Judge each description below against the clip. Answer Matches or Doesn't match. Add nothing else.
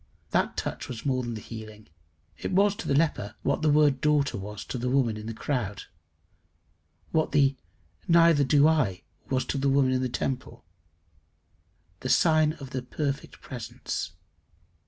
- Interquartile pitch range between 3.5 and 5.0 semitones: Matches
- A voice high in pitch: Doesn't match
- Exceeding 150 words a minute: Matches